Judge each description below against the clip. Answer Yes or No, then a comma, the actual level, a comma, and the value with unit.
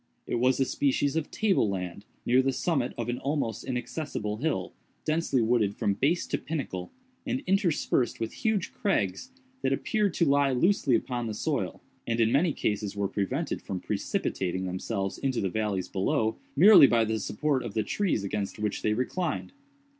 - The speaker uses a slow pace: No, average, 175 wpm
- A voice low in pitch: Yes, low, 125 Hz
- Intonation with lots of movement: Yes, wide, 6.6 semitones